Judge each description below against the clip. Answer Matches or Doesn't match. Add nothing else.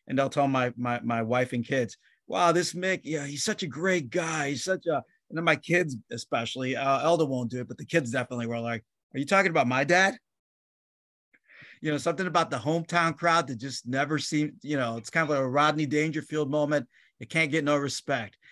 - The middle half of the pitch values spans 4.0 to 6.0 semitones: Matches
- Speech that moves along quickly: Matches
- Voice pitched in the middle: Matches